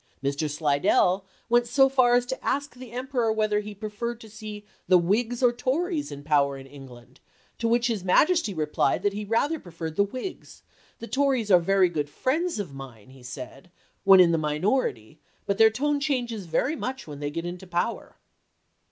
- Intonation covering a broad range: Yes, wide, 7.8 semitones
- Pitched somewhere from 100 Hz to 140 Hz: No, high, 210 Hz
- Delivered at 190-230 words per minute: Yes, average, 195 wpm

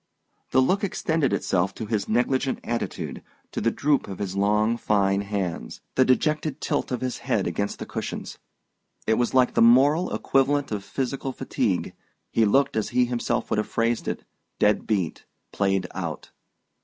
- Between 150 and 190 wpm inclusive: Yes, average, 170 wpm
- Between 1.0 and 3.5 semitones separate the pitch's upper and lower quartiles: No, average, 4.4 semitones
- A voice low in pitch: Yes, low, 120 Hz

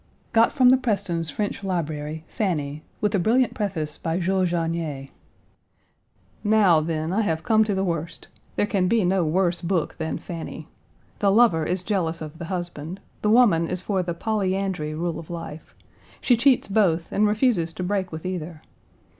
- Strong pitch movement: No, average, 3.9 semitones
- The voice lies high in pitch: No, medium, 180 Hz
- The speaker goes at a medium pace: Yes, average, 170 wpm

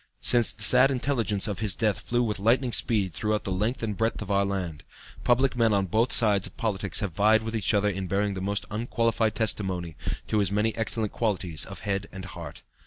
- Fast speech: Yes, fast, 215 wpm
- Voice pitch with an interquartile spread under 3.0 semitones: Yes, narrow, 2.5 semitones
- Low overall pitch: Yes, low, 105 Hz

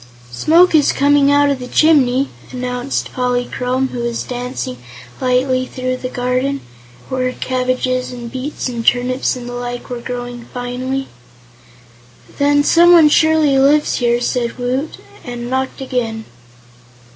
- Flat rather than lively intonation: Yes, narrow, 1.9 semitones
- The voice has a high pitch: Yes, very high, 255 Hz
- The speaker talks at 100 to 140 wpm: Yes, slow, 135 wpm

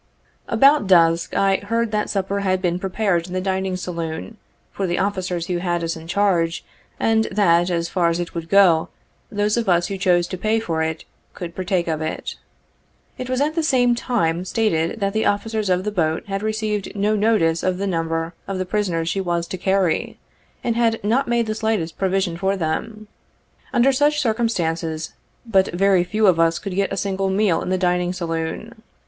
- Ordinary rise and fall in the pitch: Yes, average, 3.9 semitones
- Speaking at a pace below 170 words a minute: No, average, 195 wpm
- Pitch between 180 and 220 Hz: Yes, high, 190 Hz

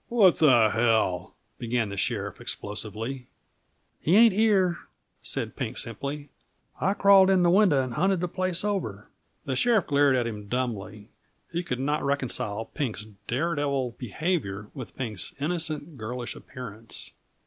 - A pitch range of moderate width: No, wide, 7.5 semitones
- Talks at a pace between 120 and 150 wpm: Yes, average, 140 wpm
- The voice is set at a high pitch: No, low, 135 Hz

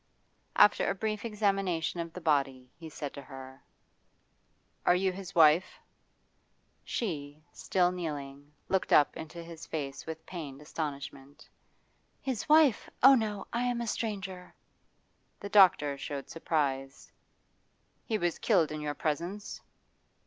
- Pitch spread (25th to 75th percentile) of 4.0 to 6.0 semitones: Yes, average, 5.2 semitones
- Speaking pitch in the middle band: Yes, medium, 165 Hz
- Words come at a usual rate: No, slow, 130 wpm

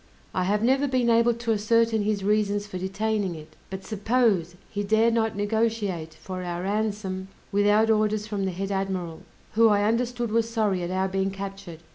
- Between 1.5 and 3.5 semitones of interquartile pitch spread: Yes, average, 2.7 semitones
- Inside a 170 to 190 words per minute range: Yes, average, 180 wpm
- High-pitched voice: Yes, high, 205 Hz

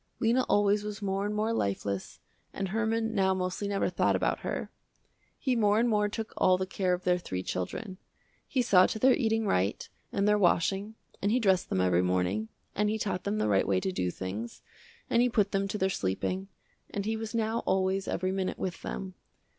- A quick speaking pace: Yes, fast, 210 wpm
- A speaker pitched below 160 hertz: No, high, 195 Hz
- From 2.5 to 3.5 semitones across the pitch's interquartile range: Yes, average, 3.2 semitones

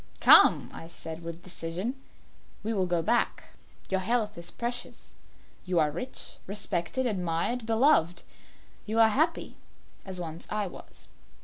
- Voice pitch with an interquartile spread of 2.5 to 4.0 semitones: No, average, 5.0 semitones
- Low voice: No, high, 190 Hz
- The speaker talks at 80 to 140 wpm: Yes, slow, 135 wpm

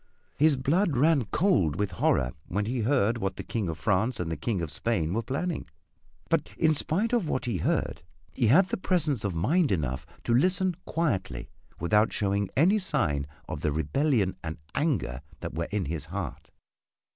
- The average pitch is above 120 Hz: No, low, 115 Hz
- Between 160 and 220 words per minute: Yes, average, 180 wpm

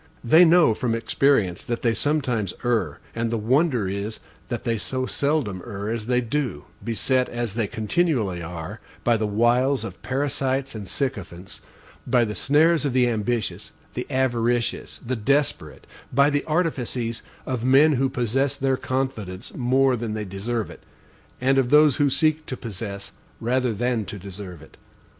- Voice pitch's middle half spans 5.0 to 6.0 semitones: No, average, 3.9 semitones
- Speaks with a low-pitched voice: Yes, low, 120 Hz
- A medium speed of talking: Yes, average, 160 wpm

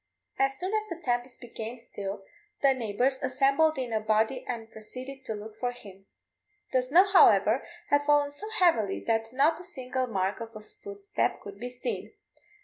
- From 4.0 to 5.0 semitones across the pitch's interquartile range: Yes, average, 4.3 semitones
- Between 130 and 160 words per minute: No, average, 175 wpm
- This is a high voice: Yes, very high, 250 Hz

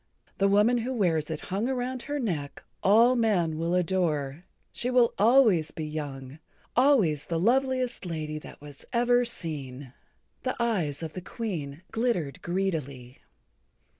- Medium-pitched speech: Yes, medium, 180 Hz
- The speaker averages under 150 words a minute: Yes, average, 140 wpm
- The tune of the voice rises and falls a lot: Yes, wide, 7.6 semitones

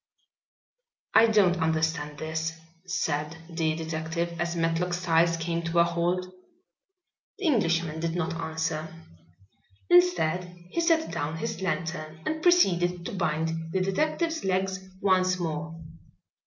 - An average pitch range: No, narrow, 2.2 semitones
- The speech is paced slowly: Yes, slow, 125 wpm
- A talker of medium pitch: Yes, medium, 170 Hz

